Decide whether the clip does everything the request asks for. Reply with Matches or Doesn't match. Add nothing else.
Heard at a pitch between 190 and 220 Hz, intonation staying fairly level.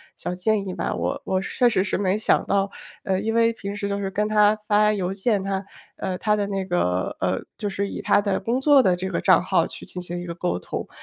Matches